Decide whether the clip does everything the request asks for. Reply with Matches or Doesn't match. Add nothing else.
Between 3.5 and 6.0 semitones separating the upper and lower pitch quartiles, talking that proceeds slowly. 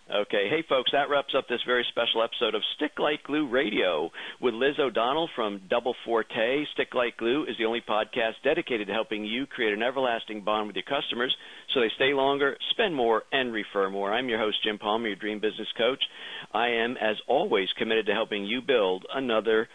Doesn't match